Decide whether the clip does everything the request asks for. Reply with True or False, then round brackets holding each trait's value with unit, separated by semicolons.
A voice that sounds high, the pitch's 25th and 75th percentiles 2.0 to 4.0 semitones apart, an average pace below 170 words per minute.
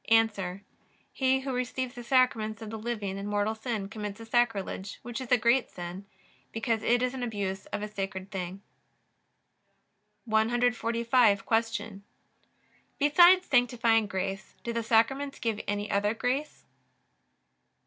True (225 Hz; 3.1 semitones; 140 wpm)